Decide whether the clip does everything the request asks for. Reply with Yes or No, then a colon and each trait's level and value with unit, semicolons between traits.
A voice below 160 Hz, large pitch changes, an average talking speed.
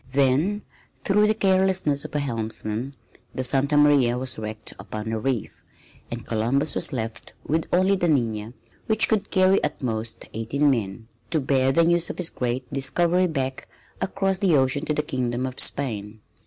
Yes: low, 135 Hz; wide, 6.2 semitones; average, 170 wpm